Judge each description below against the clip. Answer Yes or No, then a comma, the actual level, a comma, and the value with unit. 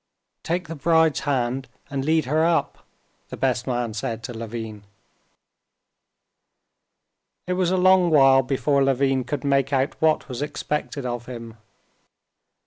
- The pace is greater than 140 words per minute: No, slow, 135 wpm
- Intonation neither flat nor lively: Yes, average, 4.2 semitones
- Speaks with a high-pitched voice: No, low, 135 Hz